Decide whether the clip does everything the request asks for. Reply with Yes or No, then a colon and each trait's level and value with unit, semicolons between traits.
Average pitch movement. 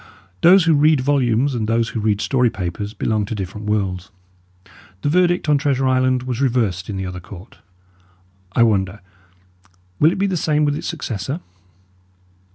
No: wide, 5.8 semitones